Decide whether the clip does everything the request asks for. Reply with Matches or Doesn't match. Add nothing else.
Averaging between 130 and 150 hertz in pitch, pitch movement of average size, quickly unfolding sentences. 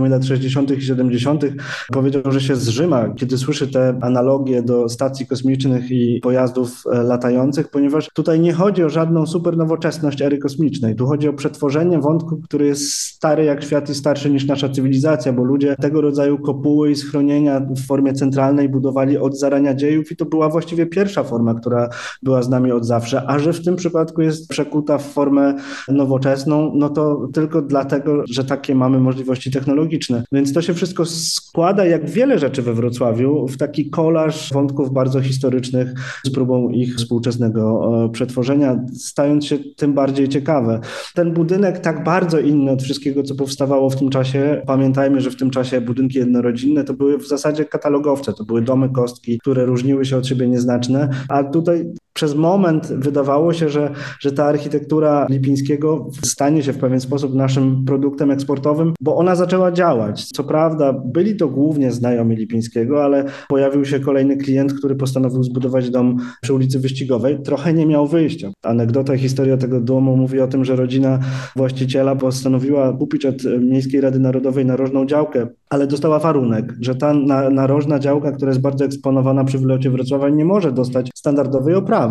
Doesn't match